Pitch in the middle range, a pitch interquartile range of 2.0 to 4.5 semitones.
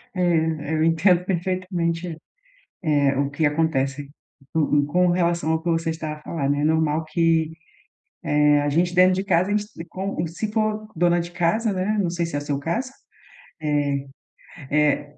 Yes: medium, 165 Hz; average, 3.2 semitones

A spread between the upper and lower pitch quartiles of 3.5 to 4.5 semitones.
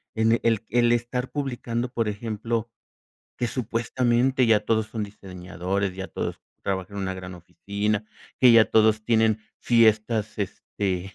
No: average, 2.8 semitones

